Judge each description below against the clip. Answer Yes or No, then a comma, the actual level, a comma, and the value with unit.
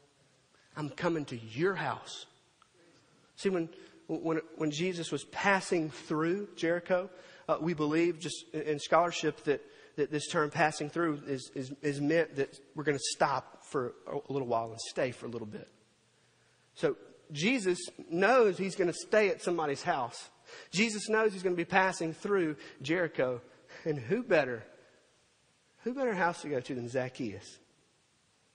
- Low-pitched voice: No, medium, 165 Hz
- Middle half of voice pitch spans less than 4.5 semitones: Yes, average, 4.0 semitones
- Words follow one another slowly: No, average, 160 wpm